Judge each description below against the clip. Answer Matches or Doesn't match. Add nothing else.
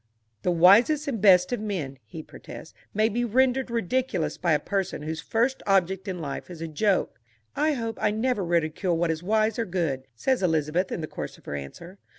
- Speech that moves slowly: Doesn't match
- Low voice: Doesn't match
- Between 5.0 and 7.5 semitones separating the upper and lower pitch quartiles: Matches